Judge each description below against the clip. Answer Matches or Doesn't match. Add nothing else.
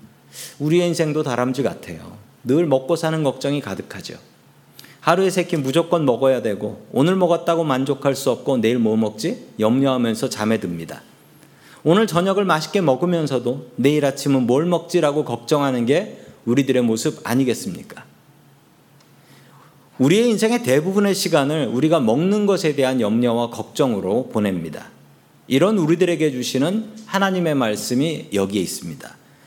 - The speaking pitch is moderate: Matches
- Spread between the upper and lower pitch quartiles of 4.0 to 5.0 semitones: Doesn't match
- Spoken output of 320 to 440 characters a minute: Matches